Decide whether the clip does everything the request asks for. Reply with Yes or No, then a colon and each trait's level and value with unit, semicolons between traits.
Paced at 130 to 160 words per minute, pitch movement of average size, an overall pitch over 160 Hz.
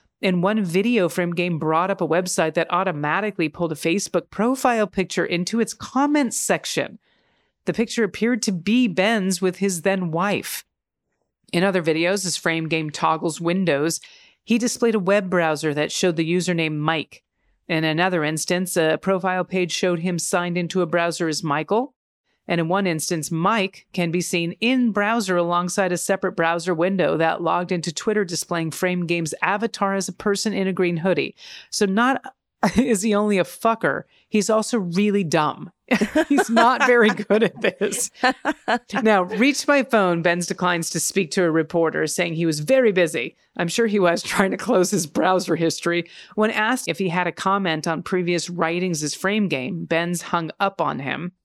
No: average, 180 wpm; average, 3.5 semitones; medium, 185 Hz